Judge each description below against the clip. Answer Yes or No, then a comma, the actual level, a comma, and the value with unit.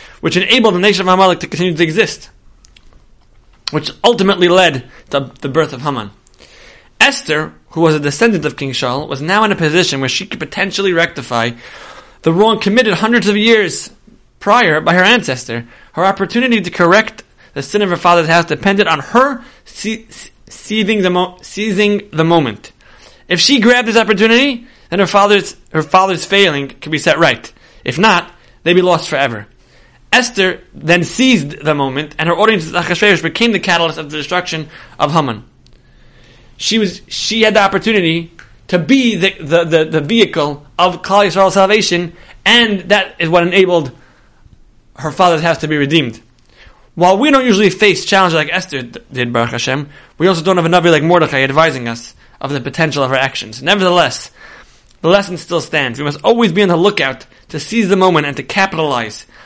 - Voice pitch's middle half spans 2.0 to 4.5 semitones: No, wide, 5.5 semitones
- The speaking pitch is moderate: Yes, medium, 175 Hz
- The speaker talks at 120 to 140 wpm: No, average, 180 wpm